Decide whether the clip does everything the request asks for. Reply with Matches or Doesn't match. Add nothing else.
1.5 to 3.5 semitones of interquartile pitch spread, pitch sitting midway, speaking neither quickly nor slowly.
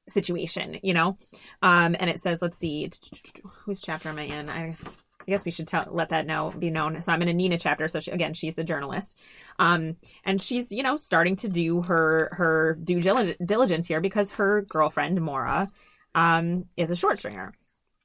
Matches